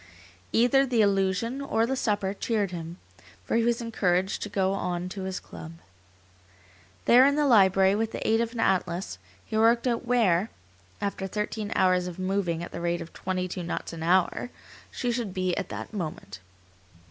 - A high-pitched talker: Yes, high, 195 Hz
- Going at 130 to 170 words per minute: No, average, 180 wpm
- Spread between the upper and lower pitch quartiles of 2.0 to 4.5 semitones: Yes, average, 4.1 semitones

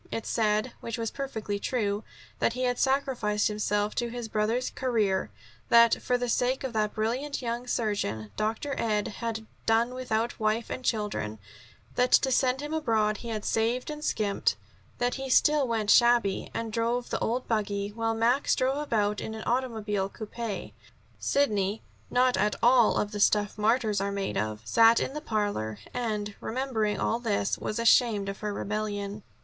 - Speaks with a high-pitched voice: Yes, high, 225 Hz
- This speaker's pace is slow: No, average, 175 wpm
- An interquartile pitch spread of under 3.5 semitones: Yes, average, 2.9 semitones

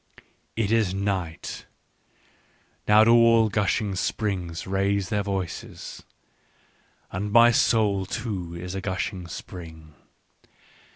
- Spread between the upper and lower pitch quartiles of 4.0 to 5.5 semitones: No, average, 2.9 semitones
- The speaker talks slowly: Yes, slow, 110 wpm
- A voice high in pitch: No, low, 100 Hz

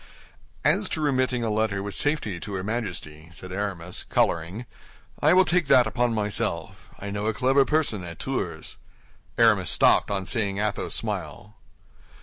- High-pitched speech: No, low, 105 Hz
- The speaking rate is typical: Yes, average, 155 wpm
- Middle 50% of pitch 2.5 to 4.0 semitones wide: No, average, 4.8 semitones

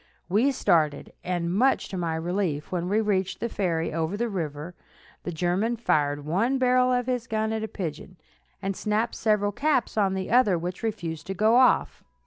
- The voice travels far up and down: No, average, 4.8 semitones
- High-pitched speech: Yes, high, 195 Hz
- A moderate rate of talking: Yes, average, 185 wpm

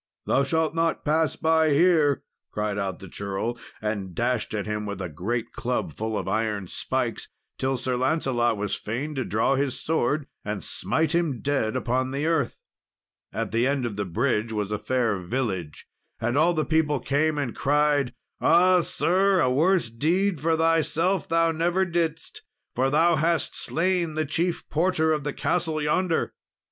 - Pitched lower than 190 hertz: Yes, medium, 140 Hz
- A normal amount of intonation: No, wide, 6.0 semitones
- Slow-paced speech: No, average, 170 wpm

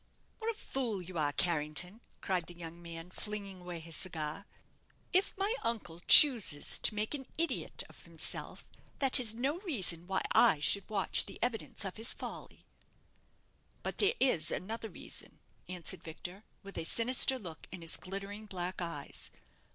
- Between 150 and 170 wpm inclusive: Yes, average, 160 wpm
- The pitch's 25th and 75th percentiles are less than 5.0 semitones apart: No, wide, 5.4 semitones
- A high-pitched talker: Yes, high, 195 Hz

